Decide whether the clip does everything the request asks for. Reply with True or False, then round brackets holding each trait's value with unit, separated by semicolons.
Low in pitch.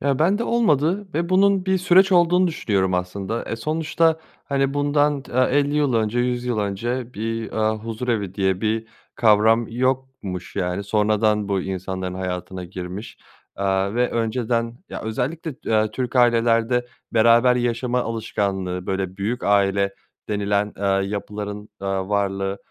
True (115 Hz)